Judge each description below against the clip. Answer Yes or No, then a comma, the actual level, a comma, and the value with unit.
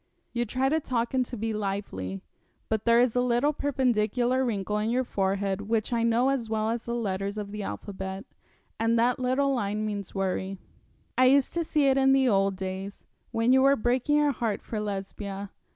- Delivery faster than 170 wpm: Yes, average, 200 wpm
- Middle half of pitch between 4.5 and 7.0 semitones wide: No, average, 4.1 semitones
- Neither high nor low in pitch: No, high, 225 Hz